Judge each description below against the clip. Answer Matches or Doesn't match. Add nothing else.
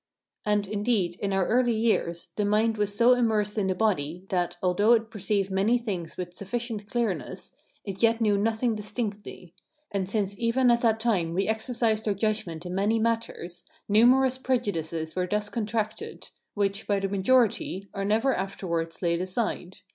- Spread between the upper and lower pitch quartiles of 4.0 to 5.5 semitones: Doesn't match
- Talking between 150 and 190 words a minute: Matches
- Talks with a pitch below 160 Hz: Doesn't match